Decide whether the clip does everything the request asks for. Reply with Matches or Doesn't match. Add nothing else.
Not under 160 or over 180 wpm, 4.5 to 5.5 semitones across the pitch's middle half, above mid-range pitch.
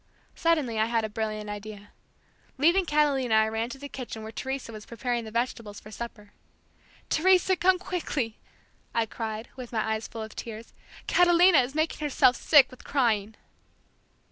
Matches